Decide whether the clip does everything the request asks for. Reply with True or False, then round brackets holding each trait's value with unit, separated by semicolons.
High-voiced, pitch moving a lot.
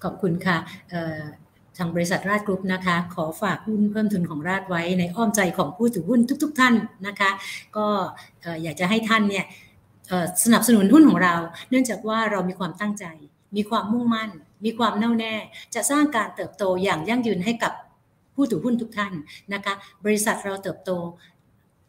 False (195 Hz; 3.9 semitones)